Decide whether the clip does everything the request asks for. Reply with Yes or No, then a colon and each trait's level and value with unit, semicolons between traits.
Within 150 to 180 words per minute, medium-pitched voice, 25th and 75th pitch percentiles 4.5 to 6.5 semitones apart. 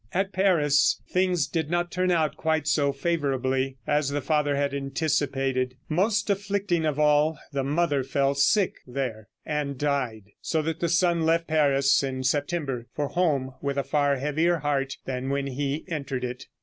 No: average, 165 wpm; medium, 145 Hz; average, 3.2 semitones